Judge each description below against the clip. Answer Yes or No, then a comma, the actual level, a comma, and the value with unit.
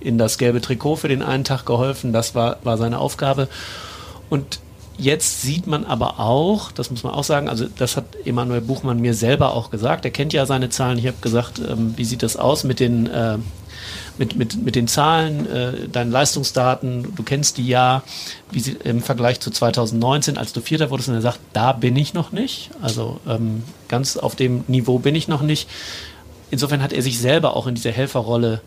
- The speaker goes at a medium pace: No, fast, 205 wpm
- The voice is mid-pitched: No, low, 125 Hz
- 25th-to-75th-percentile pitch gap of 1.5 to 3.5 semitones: Yes, average, 2.9 semitones